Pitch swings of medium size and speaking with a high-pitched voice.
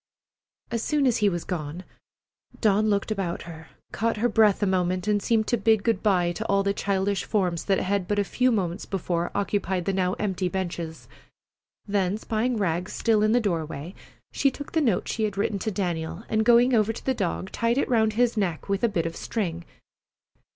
Yes: average, 3.4 semitones; high, 200 Hz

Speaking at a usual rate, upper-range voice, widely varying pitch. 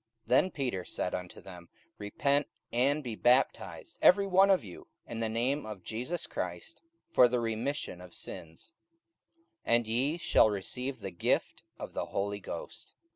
No: average, 160 wpm; low, 120 Hz; wide, 6.0 semitones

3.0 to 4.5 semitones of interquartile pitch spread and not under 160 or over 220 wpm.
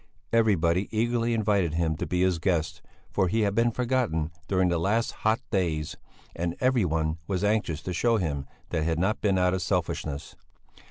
No: average, 4.9 semitones; average, 180 wpm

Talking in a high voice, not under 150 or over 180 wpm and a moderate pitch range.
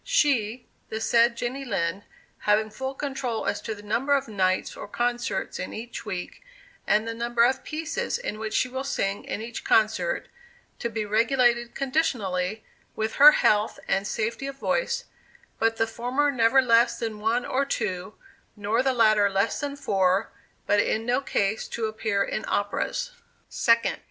Yes: high, 230 Hz; average, 165 wpm; average, 3.8 semitones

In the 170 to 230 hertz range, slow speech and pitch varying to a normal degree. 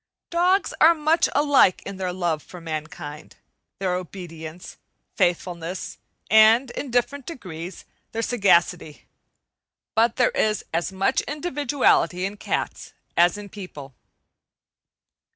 No: high, 190 Hz; slow, 115 wpm; wide, 6.3 semitones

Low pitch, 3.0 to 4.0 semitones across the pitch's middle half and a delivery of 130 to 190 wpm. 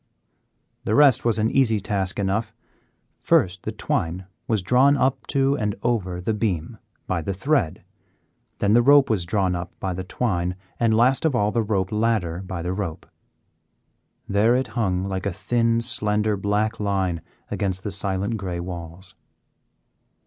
Yes: low, 100 Hz; average, 3.7 semitones; average, 160 wpm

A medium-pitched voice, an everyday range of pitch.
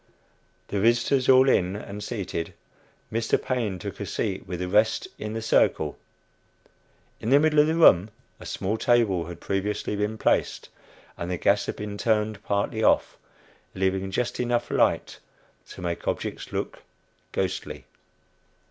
No: low, 105 Hz; average, 3.6 semitones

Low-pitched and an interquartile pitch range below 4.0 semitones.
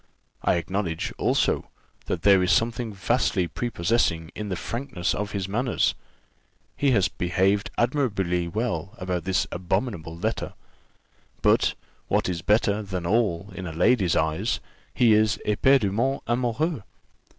No: low, 100 Hz; average, 4.8 semitones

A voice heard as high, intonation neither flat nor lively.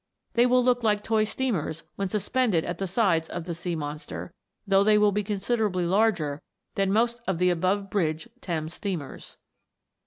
Yes: high, 195 Hz; average, 4.1 semitones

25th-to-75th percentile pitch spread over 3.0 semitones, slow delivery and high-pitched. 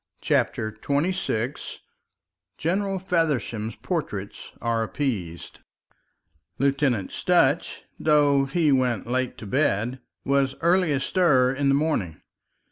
No: average, 5.1 semitones; slow, 100 wpm; low, 135 Hz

